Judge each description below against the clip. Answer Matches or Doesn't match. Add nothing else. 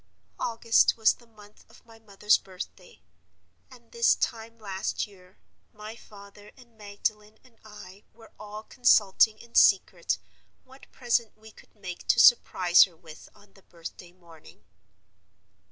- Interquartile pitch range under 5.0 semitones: Matches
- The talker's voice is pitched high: Matches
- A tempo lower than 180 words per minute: Matches